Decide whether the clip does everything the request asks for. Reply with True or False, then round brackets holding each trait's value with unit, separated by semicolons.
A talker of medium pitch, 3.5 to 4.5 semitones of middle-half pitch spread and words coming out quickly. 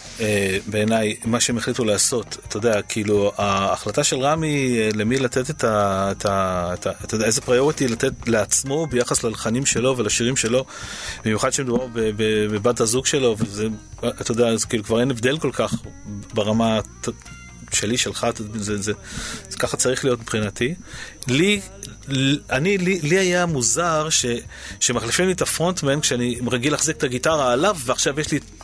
False (120 Hz; 4.2 semitones; 155 wpm)